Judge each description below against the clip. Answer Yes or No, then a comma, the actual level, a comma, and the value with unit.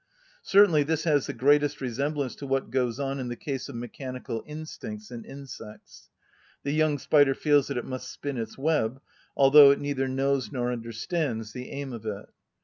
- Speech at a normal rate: Yes, average, 180 wpm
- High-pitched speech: No, low, 135 Hz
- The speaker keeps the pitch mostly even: No, average, 3.0 semitones